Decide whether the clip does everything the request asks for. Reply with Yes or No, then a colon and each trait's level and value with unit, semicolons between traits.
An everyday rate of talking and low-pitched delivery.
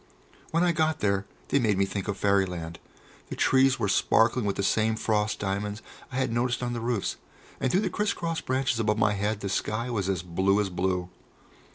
No: fast, 210 wpm; low, 105 Hz